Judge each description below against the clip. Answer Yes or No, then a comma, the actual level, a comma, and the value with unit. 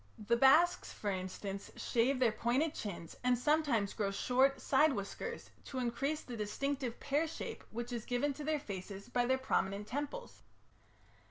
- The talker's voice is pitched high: Yes, very high, 250 Hz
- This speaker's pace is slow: No, average, 160 wpm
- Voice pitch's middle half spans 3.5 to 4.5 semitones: No, average, 5.2 semitones